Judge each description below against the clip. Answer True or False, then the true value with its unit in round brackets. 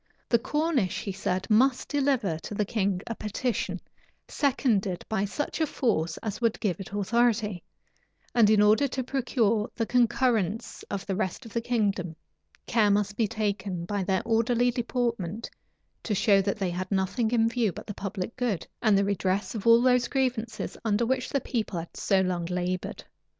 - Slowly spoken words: False (175 wpm)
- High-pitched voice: True (215 Hz)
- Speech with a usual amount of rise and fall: True (3.7 semitones)